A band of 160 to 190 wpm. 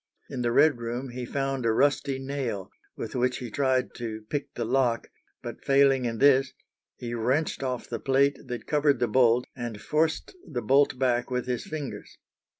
Yes: average, 180 wpm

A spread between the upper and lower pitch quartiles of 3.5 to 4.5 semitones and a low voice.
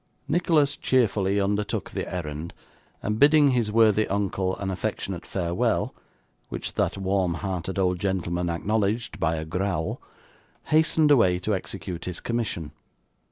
Yes: average, 3.8 semitones; very low, 95 Hz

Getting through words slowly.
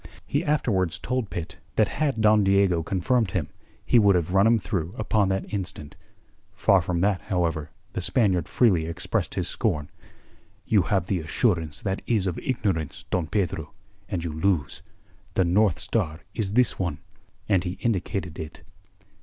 No: average, 160 wpm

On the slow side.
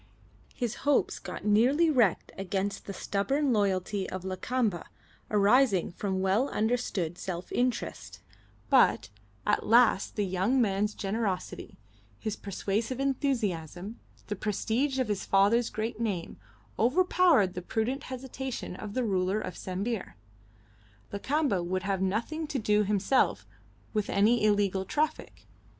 Yes: slow, 125 wpm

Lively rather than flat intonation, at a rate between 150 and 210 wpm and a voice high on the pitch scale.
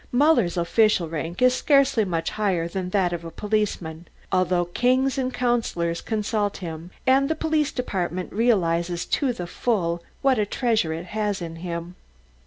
Yes: wide, 6.2 semitones; average, 160 wpm; high, 195 Hz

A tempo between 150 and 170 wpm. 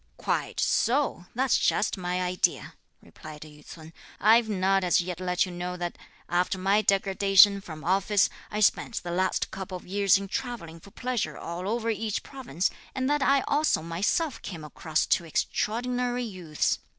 Yes: average, 165 wpm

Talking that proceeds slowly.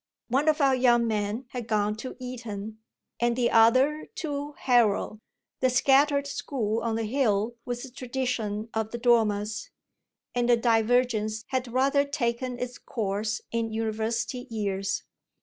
No: average, 145 wpm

